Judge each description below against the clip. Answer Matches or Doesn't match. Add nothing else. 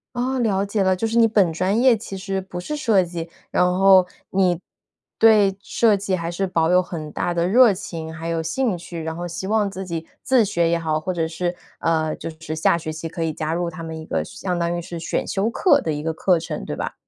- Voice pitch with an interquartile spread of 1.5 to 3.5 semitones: Matches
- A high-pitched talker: Doesn't match